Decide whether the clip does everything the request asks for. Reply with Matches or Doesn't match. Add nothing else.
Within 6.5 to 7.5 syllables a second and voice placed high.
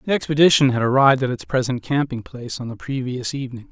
Doesn't match